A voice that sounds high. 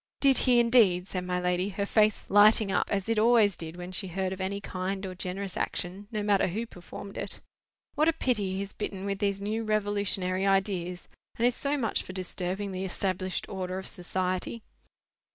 Yes: high, 195 Hz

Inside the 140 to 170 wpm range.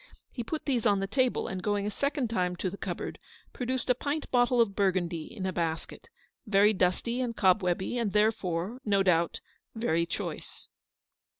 No: average, 180 wpm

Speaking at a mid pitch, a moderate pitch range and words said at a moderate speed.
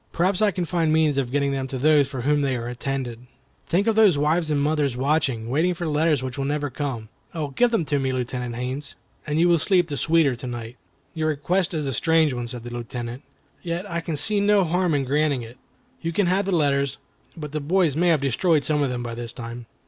No: medium, 145 Hz; average, 4.5 semitones; fast, 240 wpm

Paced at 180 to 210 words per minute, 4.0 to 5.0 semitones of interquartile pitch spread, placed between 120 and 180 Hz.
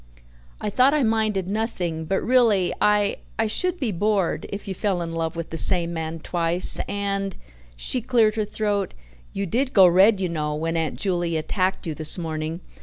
No: average, 185 wpm; average, 4.3 semitones; high, 190 Hz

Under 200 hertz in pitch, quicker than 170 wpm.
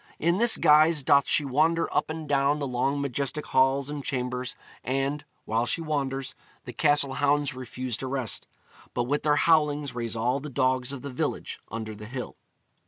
Yes: medium, 140 Hz; average, 180 wpm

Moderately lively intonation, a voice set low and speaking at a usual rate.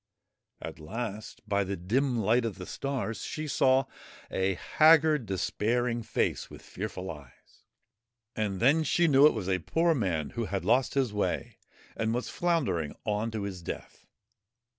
No: wide, 5.7 semitones; low, 110 Hz; average, 160 wpm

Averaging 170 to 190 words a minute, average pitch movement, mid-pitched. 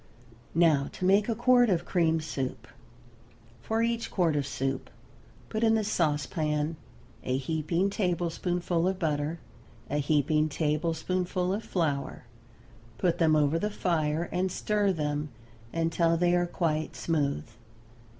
No: slow, 135 wpm; average, 3.3 semitones; medium, 165 Hz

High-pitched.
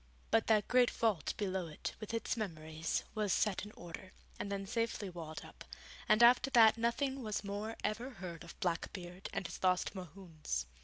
Yes: high, 200 Hz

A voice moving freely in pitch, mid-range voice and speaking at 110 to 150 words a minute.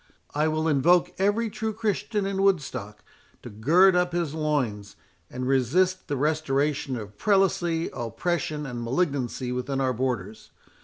Yes: wide, 6.1 semitones; medium, 150 Hz; average, 140 wpm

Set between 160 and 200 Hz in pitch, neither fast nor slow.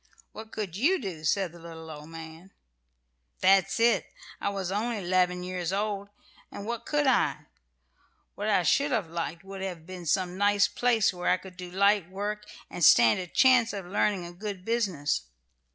Yes: high, 190 Hz; average, 185 wpm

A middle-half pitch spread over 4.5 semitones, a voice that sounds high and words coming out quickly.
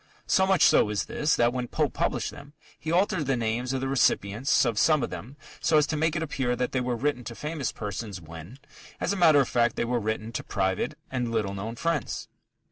No: average, 5.0 semitones; low, 125 Hz; fast, 230 wpm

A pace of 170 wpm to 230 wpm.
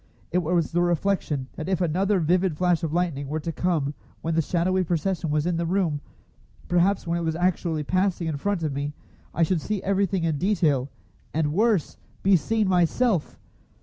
Yes: average, 185 wpm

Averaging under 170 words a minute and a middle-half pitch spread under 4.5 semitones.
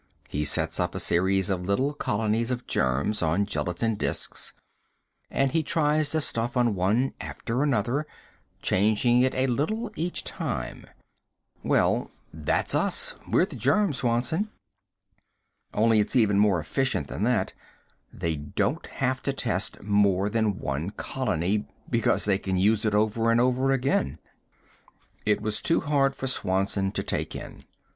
No: average, 150 wpm; average, 5.1 semitones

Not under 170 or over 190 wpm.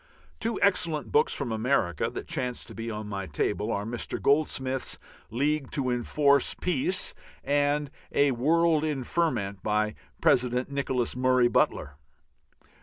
No: slow, 135 wpm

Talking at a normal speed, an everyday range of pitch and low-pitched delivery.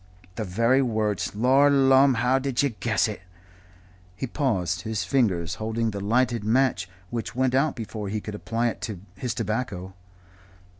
Yes: average, 160 wpm; average, 3.7 semitones; low, 115 Hz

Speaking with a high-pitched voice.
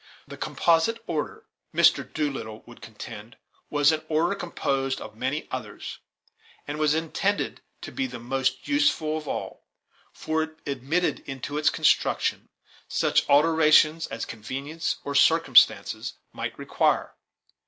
No: medium, 150 Hz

